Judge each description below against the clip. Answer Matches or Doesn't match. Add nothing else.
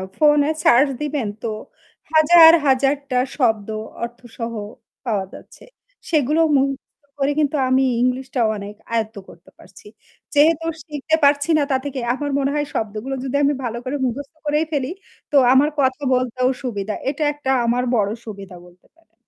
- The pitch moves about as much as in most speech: Matches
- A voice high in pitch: Matches